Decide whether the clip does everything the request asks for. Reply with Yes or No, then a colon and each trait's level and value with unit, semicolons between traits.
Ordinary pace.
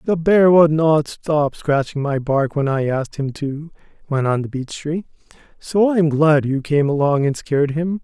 No: fast, 210 wpm